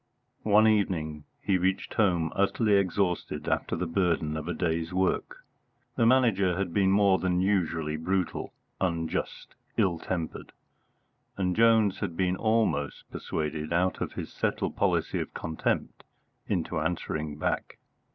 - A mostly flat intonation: No, average, 3.4 semitones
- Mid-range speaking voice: No, very low, 90 Hz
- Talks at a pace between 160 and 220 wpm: No, slow, 135 wpm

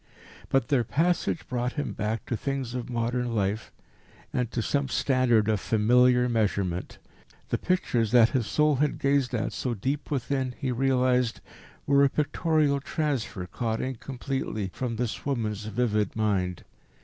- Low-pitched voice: Yes, low, 125 Hz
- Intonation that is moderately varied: Yes, average, 3.7 semitones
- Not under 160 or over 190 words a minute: No, average, 150 wpm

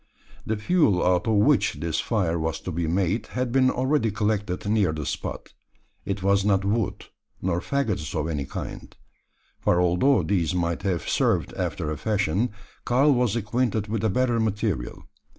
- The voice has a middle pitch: No, low, 100 Hz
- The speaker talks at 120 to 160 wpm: No, average, 170 wpm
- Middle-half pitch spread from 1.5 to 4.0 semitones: No, average, 4.5 semitones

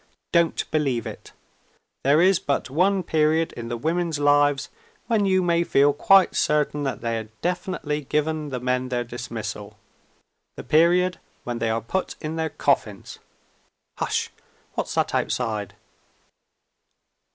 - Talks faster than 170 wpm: No, average, 140 wpm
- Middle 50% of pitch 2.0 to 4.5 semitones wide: No, average, 5.1 semitones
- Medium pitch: Yes, medium, 150 Hz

